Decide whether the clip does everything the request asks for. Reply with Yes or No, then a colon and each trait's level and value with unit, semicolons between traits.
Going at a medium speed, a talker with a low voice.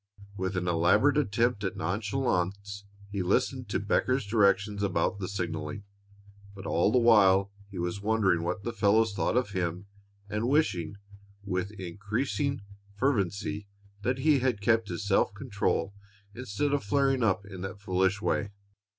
Yes: average, 150 wpm; low, 100 Hz